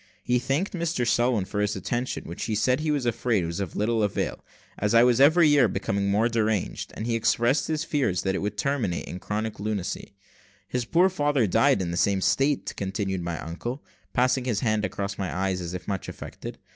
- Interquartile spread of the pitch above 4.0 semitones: Yes, average, 4.6 semitones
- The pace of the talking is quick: Yes, fast, 210 wpm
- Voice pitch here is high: No, low, 110 Hz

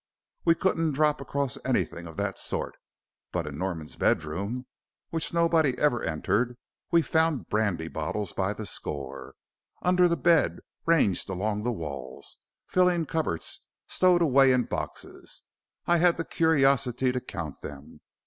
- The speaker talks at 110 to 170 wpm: Yes, average, 140 wpm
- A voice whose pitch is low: Yes, low, 125 Hz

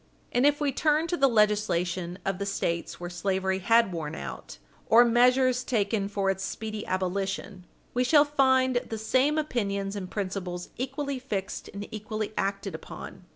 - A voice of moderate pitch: No, high, 210 Hz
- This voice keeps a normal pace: Yes, average, 160 wpm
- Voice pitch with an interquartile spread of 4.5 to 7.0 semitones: Yes, average, 4.8 semitones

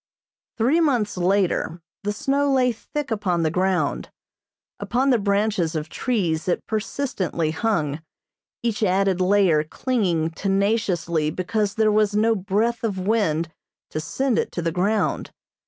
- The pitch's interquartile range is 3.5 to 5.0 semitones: Yes, average, 4.5 semitones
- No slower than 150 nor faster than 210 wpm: No, average, 140 wpm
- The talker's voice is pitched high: Yes, high, 200 Hz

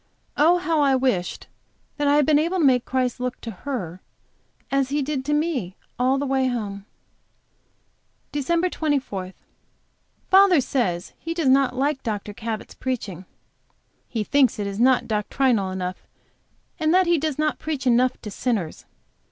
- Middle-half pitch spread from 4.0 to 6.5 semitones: Yes, wide, 5.4 semitones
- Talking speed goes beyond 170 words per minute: No, average, 160 wpm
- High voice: Yes, very high, 260 Hz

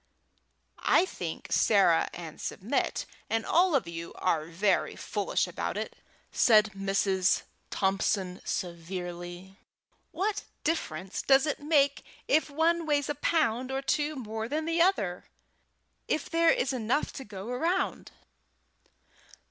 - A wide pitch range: Yes, wide, 8.2 semitones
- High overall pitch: Yes, high, 240 Hz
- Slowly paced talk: Yes, slow, 125 wpm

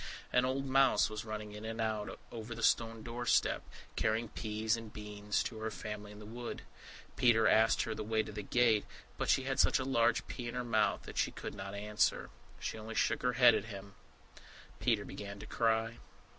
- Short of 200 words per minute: No, fast, 205 wpm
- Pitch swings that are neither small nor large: No, narrow, 1.9 semitones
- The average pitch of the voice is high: No, low, 110 Hz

